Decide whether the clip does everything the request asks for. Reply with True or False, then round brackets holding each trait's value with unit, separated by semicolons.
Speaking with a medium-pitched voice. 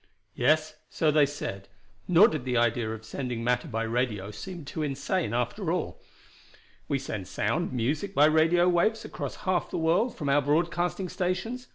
True (155 Hz)